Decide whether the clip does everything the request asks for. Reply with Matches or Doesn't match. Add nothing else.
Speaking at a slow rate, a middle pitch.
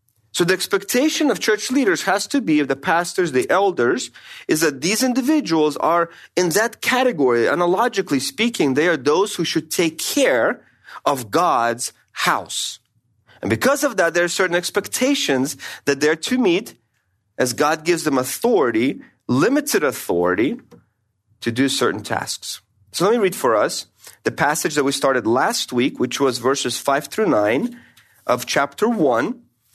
Doesn't match